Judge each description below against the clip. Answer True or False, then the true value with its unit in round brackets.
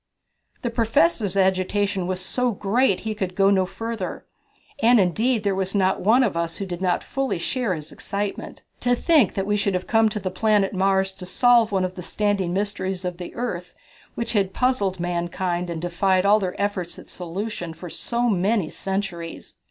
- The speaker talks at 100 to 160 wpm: False (190 wpm)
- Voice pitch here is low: False (195 Hz)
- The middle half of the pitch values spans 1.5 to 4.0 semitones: True (3.2 semitones)